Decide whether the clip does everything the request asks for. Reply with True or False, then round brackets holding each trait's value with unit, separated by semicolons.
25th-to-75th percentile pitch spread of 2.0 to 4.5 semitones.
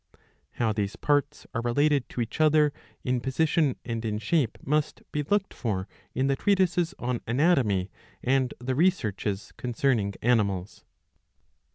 False (5.1 semitones)